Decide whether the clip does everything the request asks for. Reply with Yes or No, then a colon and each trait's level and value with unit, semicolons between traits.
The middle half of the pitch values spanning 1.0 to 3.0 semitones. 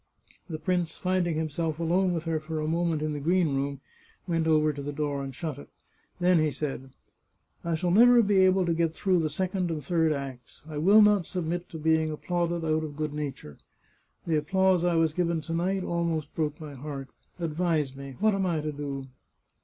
Yes: average, 2.7 semitones